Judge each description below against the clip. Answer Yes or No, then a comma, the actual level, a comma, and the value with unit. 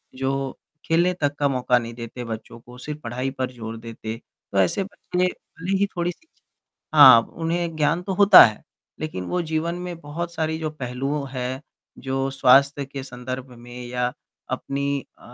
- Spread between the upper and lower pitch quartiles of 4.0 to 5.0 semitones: Yes, average, 4.7 semitones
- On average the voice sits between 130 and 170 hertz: Yes, low, 135 Hz